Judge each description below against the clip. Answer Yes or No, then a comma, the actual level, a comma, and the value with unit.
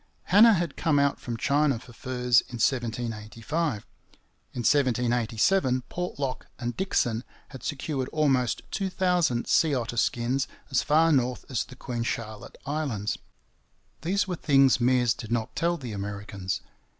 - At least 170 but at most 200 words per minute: No, average, 140 wpm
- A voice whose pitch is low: Yes, low, 130 Hz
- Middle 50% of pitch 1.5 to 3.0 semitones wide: No, average, 4.4 semitones